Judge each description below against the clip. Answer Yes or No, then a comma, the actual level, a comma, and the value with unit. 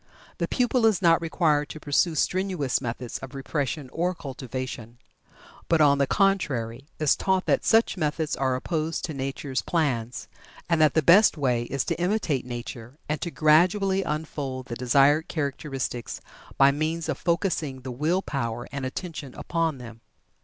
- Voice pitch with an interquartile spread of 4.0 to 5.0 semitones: Yes, average, 4.4 semitones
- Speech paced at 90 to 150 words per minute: No, average, 160 wpm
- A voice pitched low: No, medium, 145 Hz